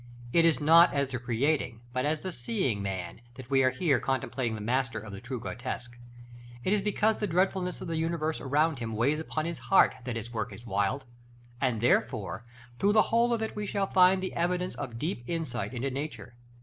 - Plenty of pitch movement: Yes, wide, 6.2 semitones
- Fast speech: Yes, fast, 210 wpm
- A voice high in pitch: No, low, 135 Hz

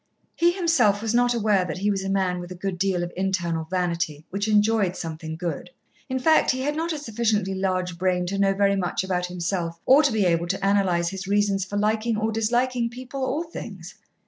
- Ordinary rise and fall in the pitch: Yes, average, 4.0 semitones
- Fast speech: Yes, fast, 215 wpm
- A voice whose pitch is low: No, high, 195 Hz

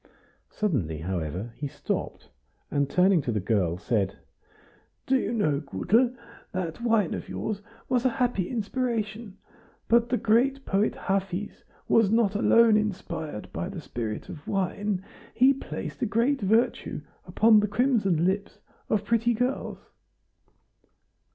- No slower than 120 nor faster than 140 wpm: Yes, slow, 135 wpm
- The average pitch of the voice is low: No, high, 205 Hz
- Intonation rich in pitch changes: Yes, wide, 6.4 semitones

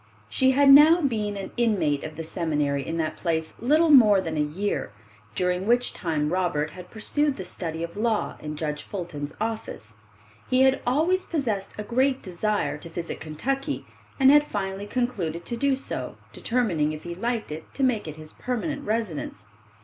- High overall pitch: Yes, high, 200 Hz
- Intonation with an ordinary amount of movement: No, wide, 7.9 semitones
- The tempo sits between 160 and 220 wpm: Yes, average, 180 wpm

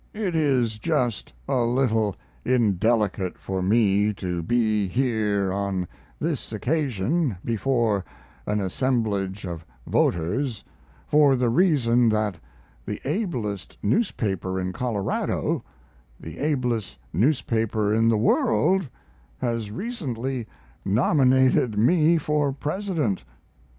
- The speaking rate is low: Yes, slow, 100 wpm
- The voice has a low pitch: Yes, low, 115 Hz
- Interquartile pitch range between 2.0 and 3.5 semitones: No, average, 4.9 semitones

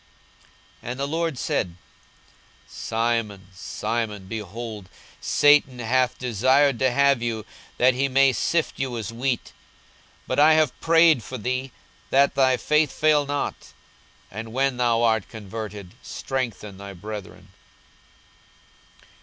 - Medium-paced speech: No, slow, 130 wpm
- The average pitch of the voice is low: Yes, low, 125 Hz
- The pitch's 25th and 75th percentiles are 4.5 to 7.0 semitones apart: No, average, 3.7 semitones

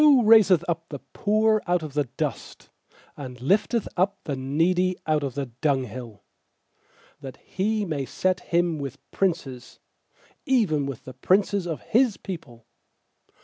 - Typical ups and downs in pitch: No, wide, 6.4 semitones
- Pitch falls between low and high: Yes, medium, 170 Hz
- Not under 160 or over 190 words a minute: No, average, 140 wpm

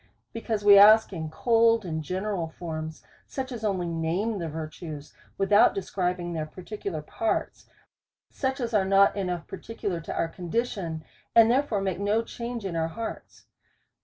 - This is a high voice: Yes, high, 195 Hz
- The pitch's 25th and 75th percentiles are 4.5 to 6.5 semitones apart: Yes, average, 5.1 semitones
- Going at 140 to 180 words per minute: Yes, average, 155 wpm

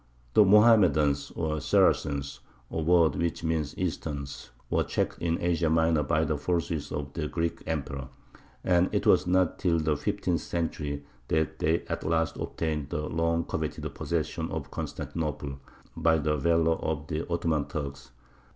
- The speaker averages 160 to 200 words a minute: No, average, 150 wpm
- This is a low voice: Yes, very low, 80 Hz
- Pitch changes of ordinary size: No, narrow, 2.1 semitones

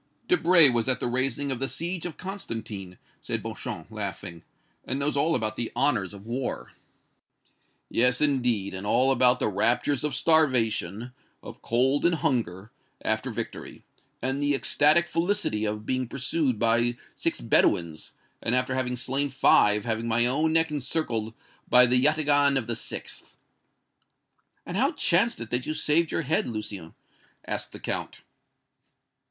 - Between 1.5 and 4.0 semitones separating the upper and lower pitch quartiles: No, average, 4.4 semitones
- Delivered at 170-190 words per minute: No, average, 155 wpm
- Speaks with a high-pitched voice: No, low, 125 Hz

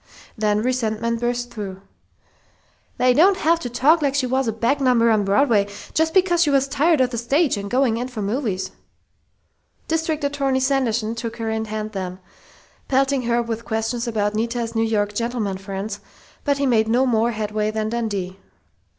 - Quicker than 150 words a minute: Yes, average, 175 wpm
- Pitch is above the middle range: Yes, high, 235 Hz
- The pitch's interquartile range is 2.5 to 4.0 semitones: Yes, average, 3.7 semitones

